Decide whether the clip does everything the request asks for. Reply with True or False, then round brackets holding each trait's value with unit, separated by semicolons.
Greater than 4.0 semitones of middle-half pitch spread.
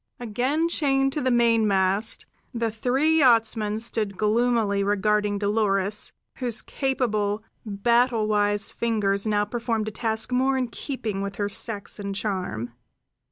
False (3.0 semitones)